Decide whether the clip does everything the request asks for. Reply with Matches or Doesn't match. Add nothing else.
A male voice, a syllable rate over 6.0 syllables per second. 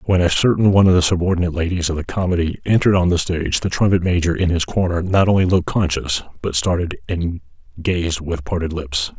Matches